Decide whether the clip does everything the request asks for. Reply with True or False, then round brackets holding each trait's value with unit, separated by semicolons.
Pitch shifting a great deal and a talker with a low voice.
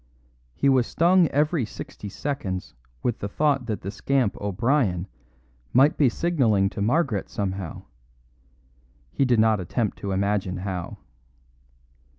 True (5.9 semitones; 110 Hz)